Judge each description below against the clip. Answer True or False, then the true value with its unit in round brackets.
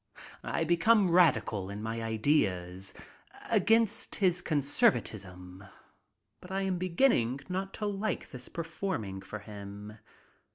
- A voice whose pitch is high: False (140 Hz)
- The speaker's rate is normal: False (115 wpm)